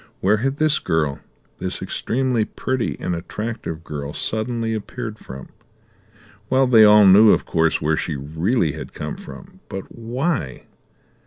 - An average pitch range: No, wide, 6.6 semitones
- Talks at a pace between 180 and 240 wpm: No, average, 145 wpm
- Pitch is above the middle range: No, low, 105 Hz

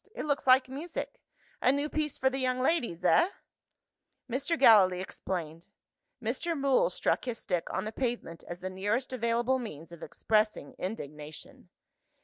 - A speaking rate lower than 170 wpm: Yes, average, 150 wpm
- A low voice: No, high, 235 Hz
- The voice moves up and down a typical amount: No, wide, 6.5 semitones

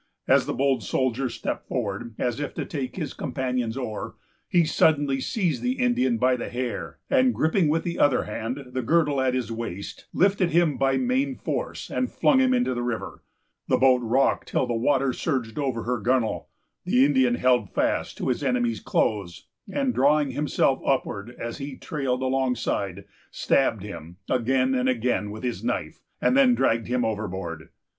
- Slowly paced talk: No, average, 175 wpm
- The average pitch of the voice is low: Yes, low, 130 Hz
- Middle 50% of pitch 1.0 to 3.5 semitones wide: No, average, 3.9 semitones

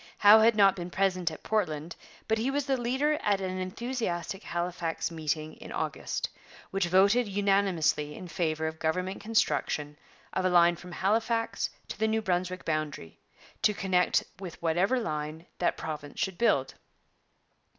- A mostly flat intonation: No, average, 4.7 semitones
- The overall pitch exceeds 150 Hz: Yes, medium, 185 Hz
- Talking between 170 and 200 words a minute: No, average, 155 wpm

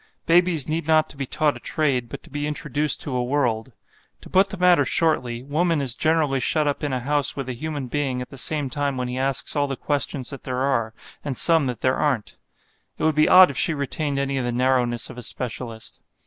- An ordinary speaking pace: No, fast, 230 wpm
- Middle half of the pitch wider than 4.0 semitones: No, average, 3.3 semitones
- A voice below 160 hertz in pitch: Yes, medium, 140 Hz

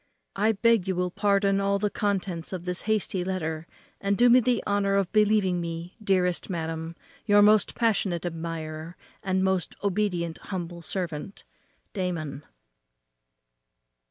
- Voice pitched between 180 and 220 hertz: Yes, medium, 185 Hz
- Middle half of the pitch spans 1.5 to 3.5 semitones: Yes, average, 3.1 semitones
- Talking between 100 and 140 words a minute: Yes, slow, 135 wpm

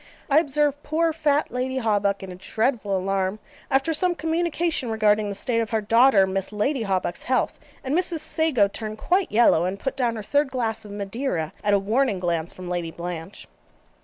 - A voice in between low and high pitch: No, high, 225 Hz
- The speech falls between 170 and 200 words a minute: Yes, average, 190 wpm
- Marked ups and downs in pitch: Yes, wide, 6.3 semitones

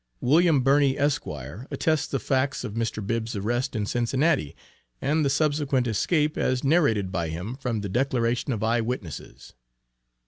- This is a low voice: Yes, low, 125 Hz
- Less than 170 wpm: Yes, average, 150 wpm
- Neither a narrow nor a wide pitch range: Yes, average, 4.5 semitones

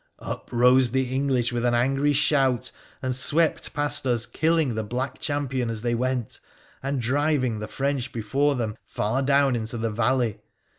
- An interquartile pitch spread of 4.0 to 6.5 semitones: No, average, 2.7 semitones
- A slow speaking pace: No, average, 165 wpm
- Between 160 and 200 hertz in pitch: No, low, 130 Hz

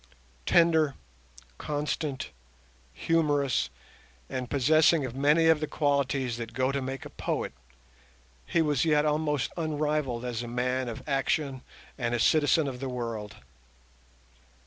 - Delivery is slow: Yes, slow, 130 wpm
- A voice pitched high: No, medium, 140 Hz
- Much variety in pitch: No, average, 3.4 semitones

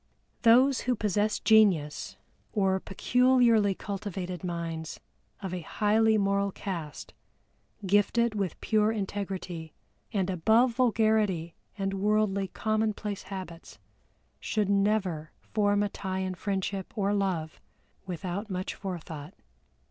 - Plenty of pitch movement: No, average, 2.8 semitones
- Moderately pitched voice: No, high, 200 Hz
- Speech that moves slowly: Yes, slow, 110 wpm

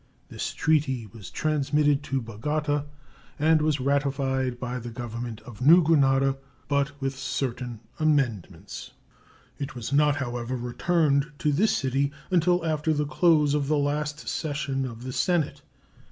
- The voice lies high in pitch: No, medium, 140 Hz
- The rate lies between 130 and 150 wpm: Yes, average, 140 wpm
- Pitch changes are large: No, average, 3.0 semitones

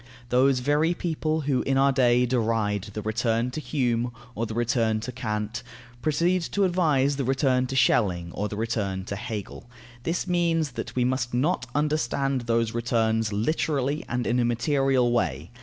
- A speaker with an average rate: Yes, average, 170 wpm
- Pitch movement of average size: Yes, average, 3.8 semitones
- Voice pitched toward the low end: Yes, low, 125 Hz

